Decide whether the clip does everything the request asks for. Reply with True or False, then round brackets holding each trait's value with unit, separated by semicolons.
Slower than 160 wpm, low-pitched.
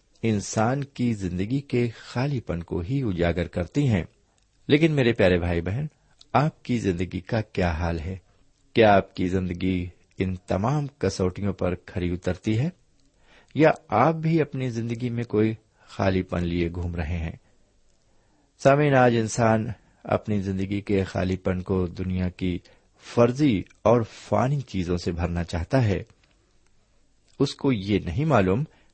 True (145 wpm; 100 Hz)